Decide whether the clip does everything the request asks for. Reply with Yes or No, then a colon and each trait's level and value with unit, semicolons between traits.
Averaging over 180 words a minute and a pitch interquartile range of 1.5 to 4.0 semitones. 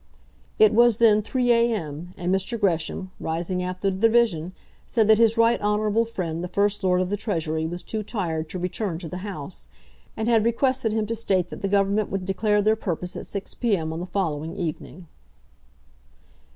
Yes: average, 190 wpm; average, 3.7 semitones